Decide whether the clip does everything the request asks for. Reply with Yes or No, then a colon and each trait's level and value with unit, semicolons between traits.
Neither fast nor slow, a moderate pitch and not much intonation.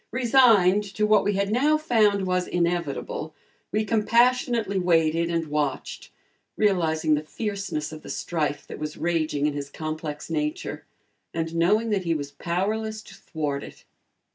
No: average, 150 wpm; medium, 180 Hz; wide, 5.5 semitones